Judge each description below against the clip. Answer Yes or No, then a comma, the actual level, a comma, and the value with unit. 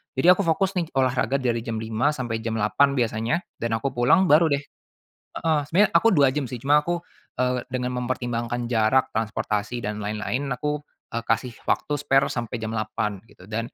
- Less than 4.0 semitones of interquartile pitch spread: No, average, 4.3 semitones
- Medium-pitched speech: No, low, 125 Hz